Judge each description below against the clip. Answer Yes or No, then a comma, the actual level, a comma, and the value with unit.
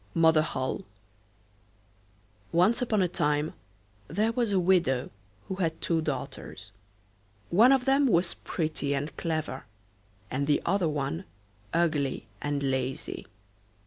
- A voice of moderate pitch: Yes, medium, 160 Hz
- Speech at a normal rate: No, slow, 115 wpm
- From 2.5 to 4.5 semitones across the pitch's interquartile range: No, average, 4.9 semitones